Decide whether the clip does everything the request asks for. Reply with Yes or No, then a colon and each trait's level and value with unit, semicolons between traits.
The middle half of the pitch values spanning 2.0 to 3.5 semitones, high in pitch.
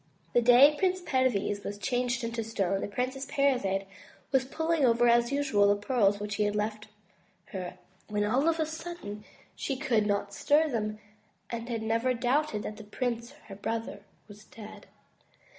No: average, 4.4 semitones; high, 235 Hz